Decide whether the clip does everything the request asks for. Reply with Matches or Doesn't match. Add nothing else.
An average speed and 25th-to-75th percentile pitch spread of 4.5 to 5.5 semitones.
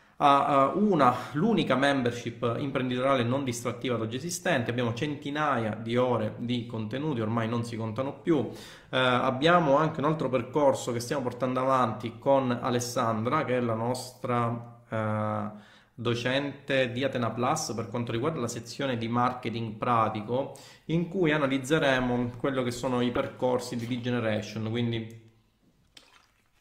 Doesn't match